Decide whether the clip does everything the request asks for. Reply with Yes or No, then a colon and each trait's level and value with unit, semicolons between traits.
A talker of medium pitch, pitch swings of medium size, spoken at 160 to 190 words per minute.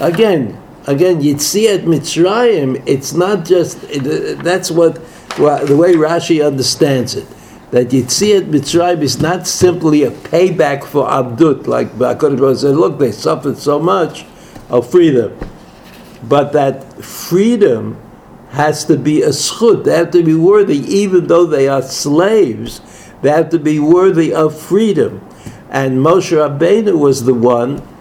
No: medium, 160 Hz; average, 3.9 semitones; average, 145 wpm